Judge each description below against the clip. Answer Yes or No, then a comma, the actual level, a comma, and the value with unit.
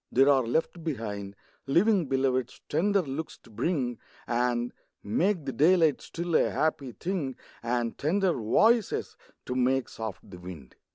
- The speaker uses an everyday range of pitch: No, wide, 5.9 semitones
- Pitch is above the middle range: No, low, 135 Hz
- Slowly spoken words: No, average, 145 wpm